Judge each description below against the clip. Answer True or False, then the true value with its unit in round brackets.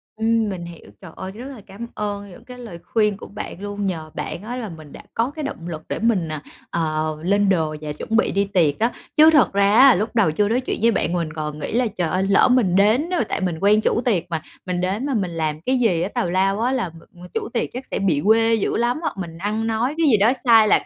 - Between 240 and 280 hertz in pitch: False (200 Hz)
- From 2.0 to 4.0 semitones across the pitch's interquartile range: False (5.0 semitones)